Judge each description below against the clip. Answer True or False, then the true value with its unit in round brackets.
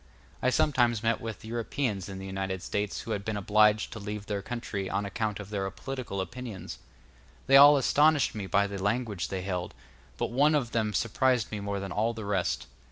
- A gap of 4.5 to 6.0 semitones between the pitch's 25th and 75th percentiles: False (3.3 semitones)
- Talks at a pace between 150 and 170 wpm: False (205 wpm)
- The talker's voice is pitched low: True (105 Hz)